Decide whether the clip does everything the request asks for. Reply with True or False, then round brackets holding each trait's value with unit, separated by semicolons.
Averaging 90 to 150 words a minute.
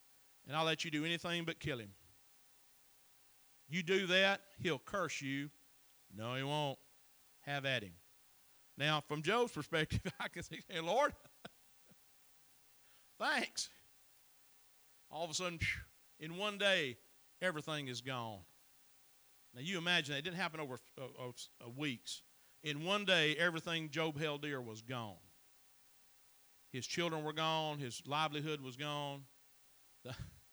True (140 wpm)